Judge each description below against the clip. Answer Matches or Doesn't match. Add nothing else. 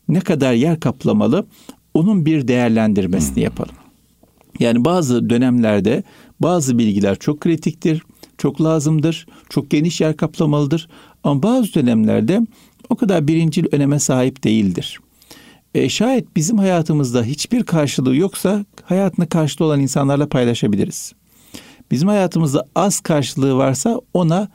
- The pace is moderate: Matches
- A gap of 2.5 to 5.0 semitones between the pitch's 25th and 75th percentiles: Doesn't match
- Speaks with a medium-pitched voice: Matches